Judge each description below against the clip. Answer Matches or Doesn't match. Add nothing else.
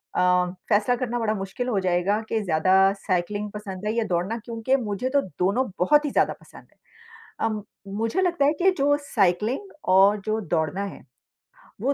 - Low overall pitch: Doesn't match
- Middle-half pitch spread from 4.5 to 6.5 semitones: Matches